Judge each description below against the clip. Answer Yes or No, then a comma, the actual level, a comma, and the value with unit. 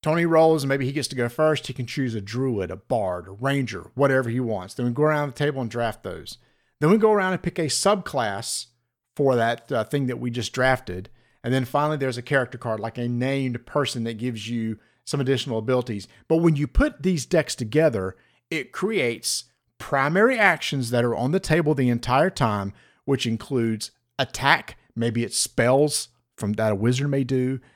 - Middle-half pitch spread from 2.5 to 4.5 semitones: Yes, average, 3.9 semitones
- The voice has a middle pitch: No, low, 130 Hz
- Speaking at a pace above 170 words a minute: Yes, fast, 205 wpm